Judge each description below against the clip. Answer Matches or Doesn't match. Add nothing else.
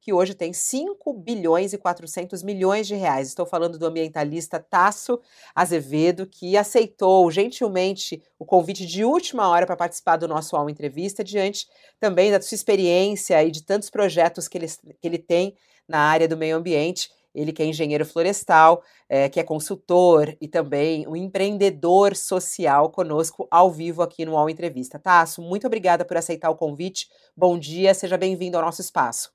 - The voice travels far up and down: Doesn't match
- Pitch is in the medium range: Matches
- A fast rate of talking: Doesn't match